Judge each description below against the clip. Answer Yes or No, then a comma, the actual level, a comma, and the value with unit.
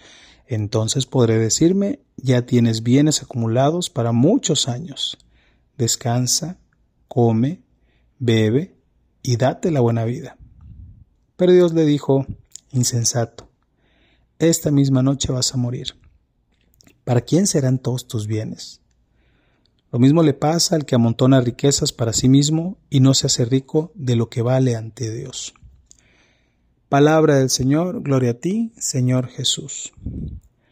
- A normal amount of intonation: Yes, average, 3.9 semitones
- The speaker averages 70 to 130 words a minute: Yes, slow, 125 wpm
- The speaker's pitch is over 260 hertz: No, low, 130 Hz